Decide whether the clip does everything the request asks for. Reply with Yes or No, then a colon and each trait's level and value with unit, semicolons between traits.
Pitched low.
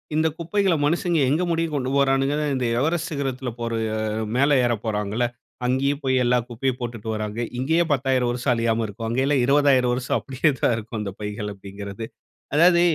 Yes: low, 130 Hz